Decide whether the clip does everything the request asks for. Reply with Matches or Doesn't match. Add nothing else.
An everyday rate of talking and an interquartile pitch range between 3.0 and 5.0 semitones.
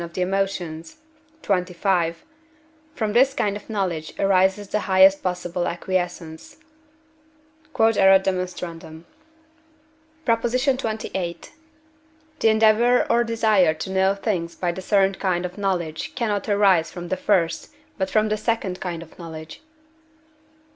Doesn't match